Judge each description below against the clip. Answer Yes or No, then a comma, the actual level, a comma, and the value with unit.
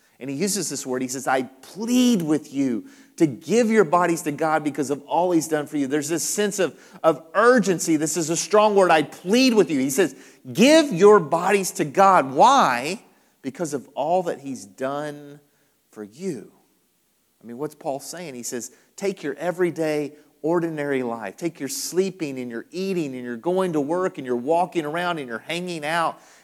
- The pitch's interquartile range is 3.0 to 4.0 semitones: No, average, 4.8 semitones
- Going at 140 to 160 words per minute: No, average, 195 wpm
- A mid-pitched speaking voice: Yes, medium, 165 Hz